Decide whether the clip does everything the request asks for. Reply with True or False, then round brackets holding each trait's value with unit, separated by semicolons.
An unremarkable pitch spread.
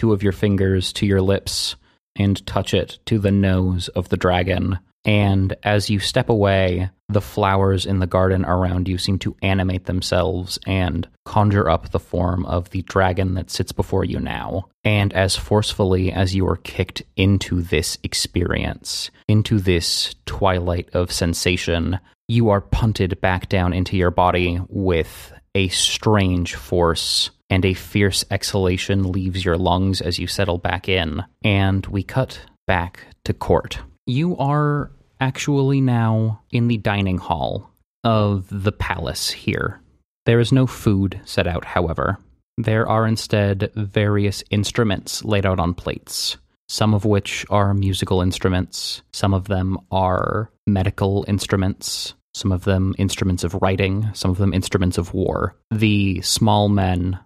False (2.2 semitones)